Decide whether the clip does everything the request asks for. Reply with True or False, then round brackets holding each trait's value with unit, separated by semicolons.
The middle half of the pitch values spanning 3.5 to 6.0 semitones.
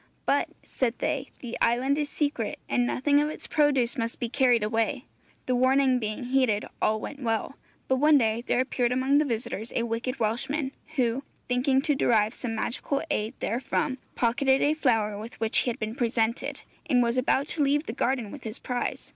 False (3.0 semitones)